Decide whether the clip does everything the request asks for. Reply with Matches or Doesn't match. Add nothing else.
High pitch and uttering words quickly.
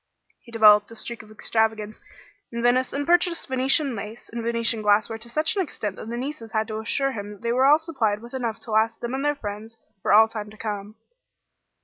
Matches